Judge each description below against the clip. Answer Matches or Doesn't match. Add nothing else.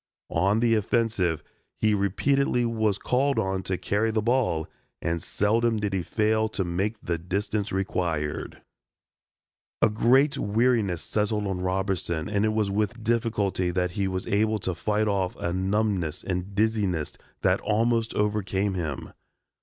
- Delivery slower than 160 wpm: Matches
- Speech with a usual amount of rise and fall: Matches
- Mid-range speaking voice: Doesn't match